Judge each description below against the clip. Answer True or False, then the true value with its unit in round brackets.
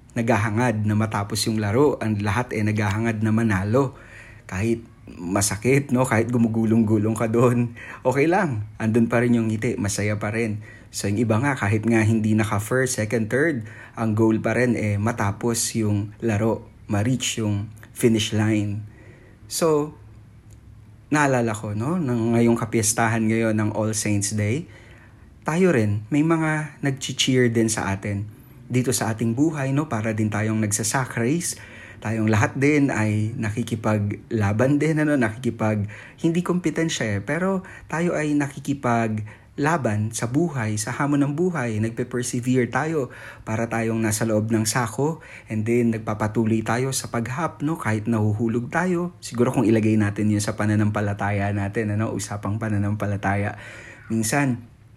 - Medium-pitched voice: False (115 Hz)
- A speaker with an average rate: True (145 wpm)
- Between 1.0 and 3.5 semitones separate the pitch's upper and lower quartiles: True (2.7 semitones)